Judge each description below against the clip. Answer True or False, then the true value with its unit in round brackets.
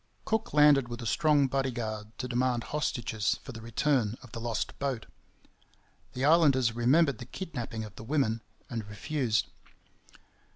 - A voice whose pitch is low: True (125 Hz)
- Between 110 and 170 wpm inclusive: True (150 wpm)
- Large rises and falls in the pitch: False (3.8 semitones)